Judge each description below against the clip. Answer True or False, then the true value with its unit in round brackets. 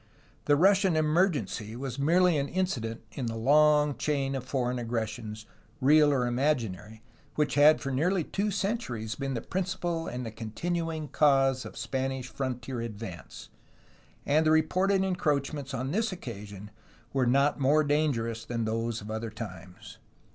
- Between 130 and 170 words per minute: True (150 wpm)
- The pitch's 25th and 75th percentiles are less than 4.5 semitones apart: False (5.1 semitones)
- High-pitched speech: False (135 Hz)